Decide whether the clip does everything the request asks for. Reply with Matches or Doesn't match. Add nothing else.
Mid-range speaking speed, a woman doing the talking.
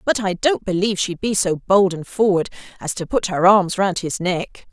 Doesn't match